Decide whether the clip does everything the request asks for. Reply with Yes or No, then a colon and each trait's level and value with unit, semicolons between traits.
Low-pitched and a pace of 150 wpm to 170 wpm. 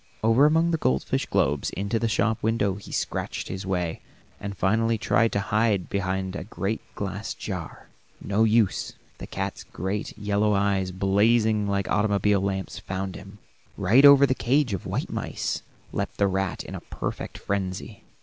Yes: low, 100 Hz; average, 165 wpm